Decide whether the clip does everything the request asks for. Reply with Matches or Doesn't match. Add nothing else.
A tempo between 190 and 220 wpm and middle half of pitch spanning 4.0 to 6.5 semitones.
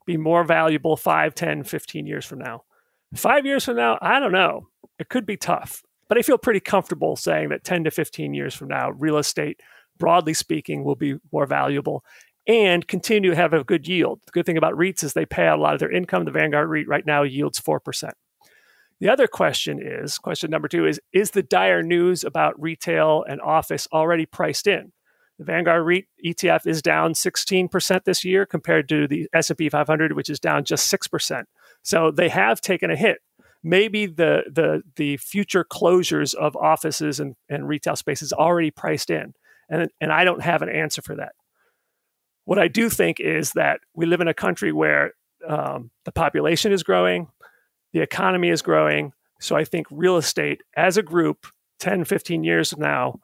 Doesn't match